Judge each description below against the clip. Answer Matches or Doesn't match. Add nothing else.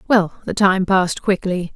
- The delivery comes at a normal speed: Matches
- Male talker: Doesn't match